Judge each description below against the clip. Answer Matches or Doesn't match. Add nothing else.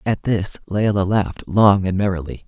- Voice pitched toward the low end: Matches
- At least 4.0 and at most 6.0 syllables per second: Matches